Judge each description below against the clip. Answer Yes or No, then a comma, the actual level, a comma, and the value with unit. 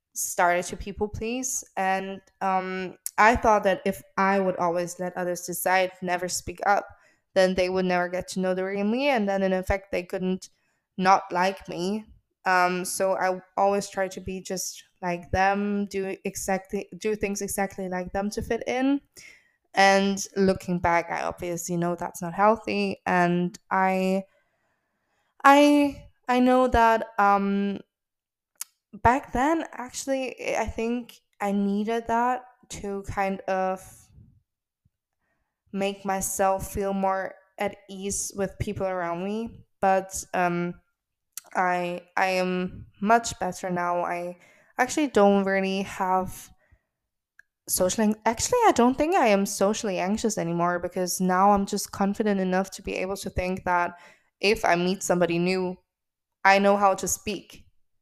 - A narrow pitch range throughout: Yes, narrow, 2.0 semitones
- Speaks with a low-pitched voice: No, high, 195 Hz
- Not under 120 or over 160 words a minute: Yes, average, 145 wpm